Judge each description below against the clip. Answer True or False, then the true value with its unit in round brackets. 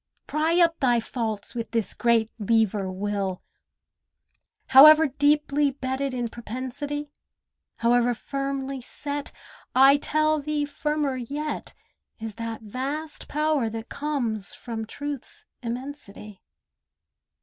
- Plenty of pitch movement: False (4.3 semitones)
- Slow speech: True (105 wpm)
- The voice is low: False (265 Hz)